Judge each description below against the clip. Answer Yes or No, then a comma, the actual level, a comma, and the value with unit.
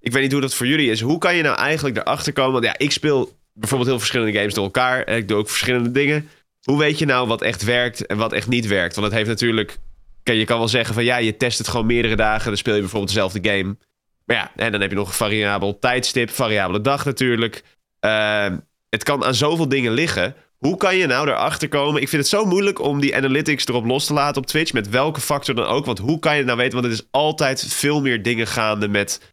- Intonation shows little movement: No, average, 4.5 semitones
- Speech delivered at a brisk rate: Yes, fast, 260 wpm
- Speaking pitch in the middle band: No, low, 125 Hz